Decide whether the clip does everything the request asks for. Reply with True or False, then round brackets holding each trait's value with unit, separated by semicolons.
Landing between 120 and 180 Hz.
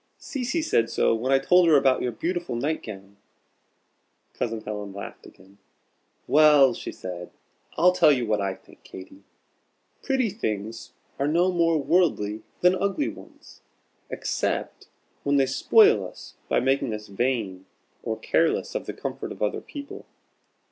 True (135 Hz)